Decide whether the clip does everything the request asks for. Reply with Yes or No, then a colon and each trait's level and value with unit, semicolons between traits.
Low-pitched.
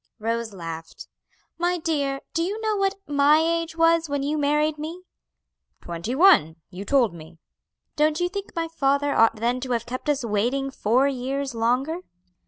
No: very high, 280 Hz